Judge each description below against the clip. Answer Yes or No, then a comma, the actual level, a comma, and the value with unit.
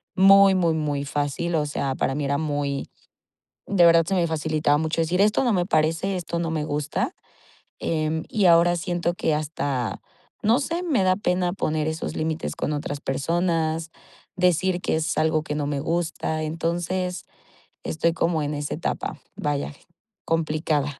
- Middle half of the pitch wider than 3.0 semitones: No, average, 2.7 semitones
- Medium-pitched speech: Yes, medium, 160 Hz